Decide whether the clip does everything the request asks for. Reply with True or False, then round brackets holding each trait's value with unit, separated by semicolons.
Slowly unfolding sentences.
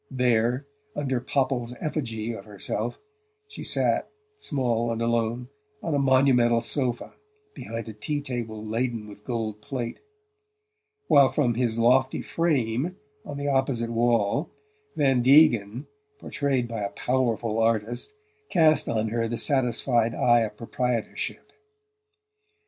True (125 wpm)